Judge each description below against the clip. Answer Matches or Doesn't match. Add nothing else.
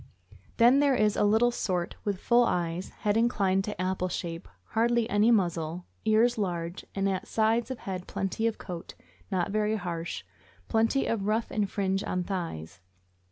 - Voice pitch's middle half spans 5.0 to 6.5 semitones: Doesn't match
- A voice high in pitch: Matches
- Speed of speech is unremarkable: Matches